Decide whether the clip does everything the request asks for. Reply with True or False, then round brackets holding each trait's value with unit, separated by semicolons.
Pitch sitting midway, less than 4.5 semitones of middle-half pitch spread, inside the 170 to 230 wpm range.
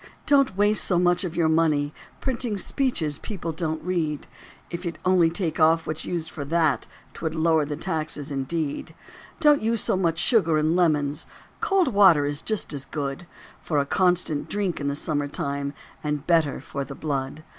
True (160 Hz; 3.7 semitones; 175 wpm)